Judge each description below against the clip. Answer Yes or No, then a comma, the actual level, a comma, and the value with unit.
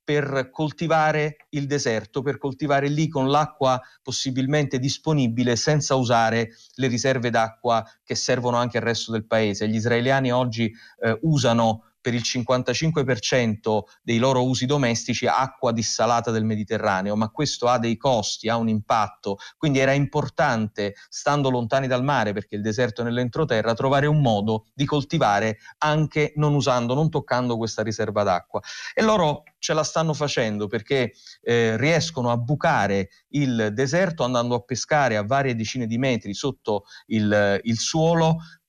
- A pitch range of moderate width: Yes, average, 4.1 semitones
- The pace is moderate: Yes, average, 150 wpm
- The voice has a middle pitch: No, low, 125 Hz